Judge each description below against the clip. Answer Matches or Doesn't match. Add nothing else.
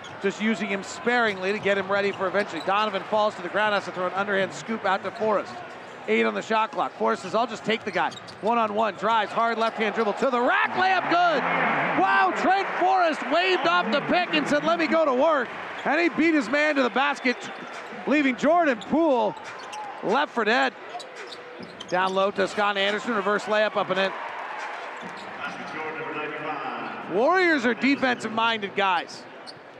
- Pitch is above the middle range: Matches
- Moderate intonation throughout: Doesn't match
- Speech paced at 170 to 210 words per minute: Matches